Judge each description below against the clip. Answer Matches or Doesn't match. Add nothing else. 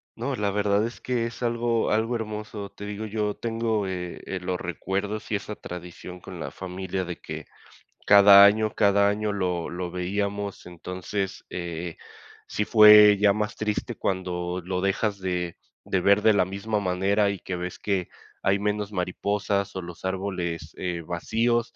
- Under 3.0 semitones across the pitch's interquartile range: Matches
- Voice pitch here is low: Matches